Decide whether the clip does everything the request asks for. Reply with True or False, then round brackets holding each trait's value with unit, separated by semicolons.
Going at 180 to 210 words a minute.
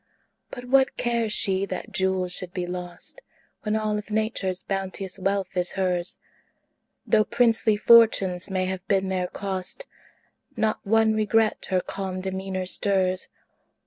False (140 wpm)